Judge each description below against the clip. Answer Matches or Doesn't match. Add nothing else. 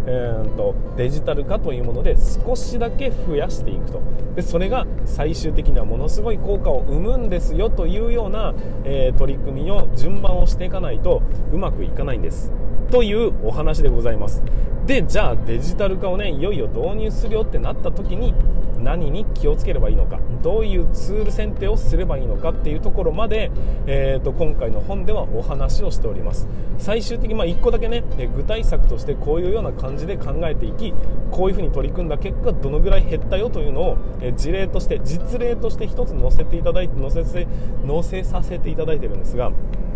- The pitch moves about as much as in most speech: Doesn't match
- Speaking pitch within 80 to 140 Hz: Matches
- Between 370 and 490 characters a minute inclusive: Matches